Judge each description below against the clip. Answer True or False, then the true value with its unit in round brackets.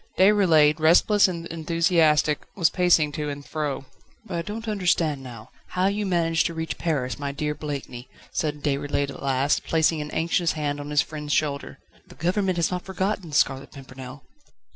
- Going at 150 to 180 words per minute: True (175 wpm)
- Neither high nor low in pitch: True (155 Hz)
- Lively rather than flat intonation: False (3.2 semitones)